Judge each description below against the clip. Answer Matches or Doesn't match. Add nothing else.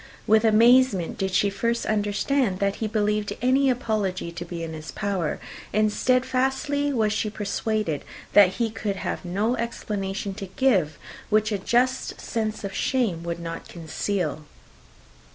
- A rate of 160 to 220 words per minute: Doesn't match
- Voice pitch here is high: Matches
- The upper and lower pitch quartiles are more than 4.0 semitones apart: Doesn't match